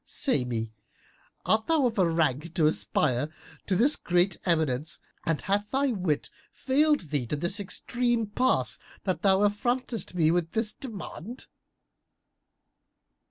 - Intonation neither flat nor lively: No, wide, 6.9 semitones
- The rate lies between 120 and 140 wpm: Yes, slow, 135 wpm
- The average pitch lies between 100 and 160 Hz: No, high, 190 Hz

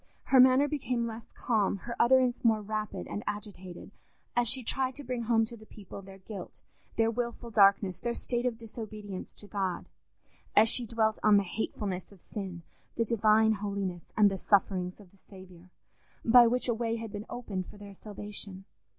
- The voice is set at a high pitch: Yes, high, 215 Hz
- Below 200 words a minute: Yes, average, 180 wpm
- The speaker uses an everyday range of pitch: Yes, average, 3.0 semitones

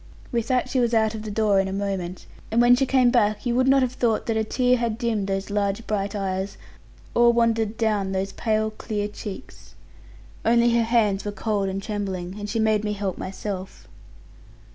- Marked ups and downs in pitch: No, average, 2.9 semitones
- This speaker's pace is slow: No, fast, 205 wpm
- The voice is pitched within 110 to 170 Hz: No, high, 215 Hz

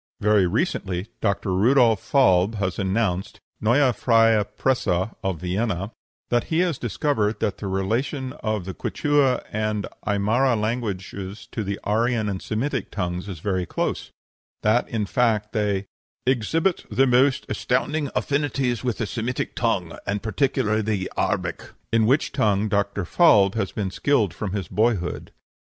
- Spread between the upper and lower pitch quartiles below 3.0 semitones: No, average, 4.0 semitones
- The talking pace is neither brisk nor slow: Yes, average, 145 wpm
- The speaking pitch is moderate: No, low, 110 Hz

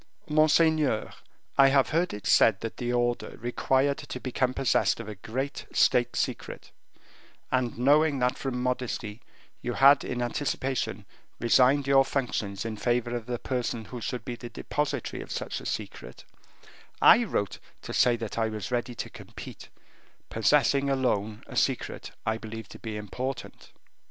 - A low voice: Yes, low, 125 Hz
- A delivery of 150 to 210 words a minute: Yes, average, 155 wpm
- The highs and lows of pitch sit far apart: No, average, 3.2 semitones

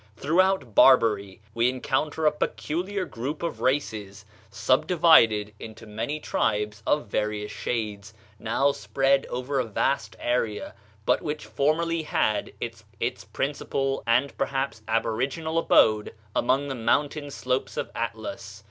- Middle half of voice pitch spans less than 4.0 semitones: No, average, 5.2 semitones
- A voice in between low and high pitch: No, low, 130 Hz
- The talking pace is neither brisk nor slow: No, slow, 120 wpm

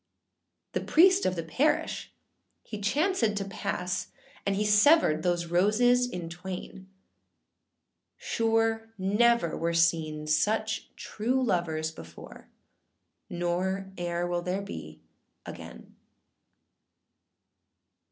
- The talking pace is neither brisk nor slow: No, slow, 100 wpm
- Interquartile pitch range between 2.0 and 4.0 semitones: No, average, 4.4 semitones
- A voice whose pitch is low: No, high, 190 Hz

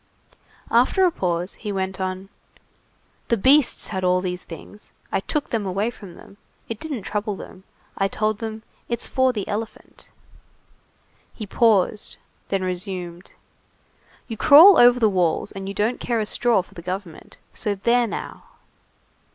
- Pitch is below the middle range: No, high, 205 Hz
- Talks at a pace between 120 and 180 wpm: Yes, average, 160 wpm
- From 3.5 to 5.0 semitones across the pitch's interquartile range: Yes, average, 3.8 semitones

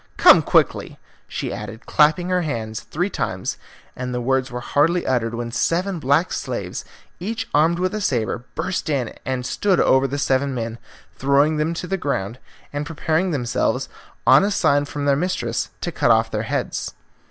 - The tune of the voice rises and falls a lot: Yes, wide, 6.0 semitones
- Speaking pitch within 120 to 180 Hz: Yes, medium, 140 Hz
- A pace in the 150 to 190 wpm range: Yes, average, 175 wpm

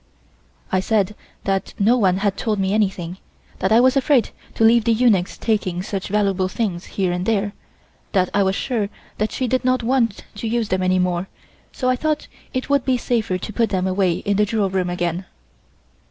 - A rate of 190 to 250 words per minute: Yes, average, 200 wpm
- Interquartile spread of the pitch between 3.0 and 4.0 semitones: Yes, average, 3.7 semitones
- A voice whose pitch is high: Yes, high, 205 Hz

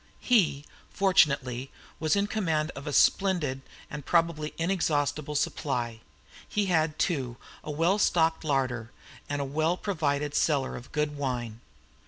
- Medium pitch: Yes, medium, 150 Hz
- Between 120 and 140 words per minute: Yes, slow, 135 wpm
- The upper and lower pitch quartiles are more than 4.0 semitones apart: No, average, 3.4 semitones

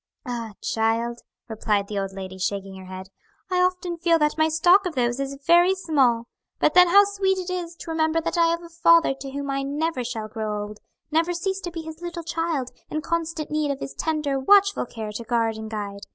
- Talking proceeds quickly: Yes, fast, 220 wpm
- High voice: Yes, very high, 300 Hz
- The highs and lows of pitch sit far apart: Yes, wide, 7.0 semitones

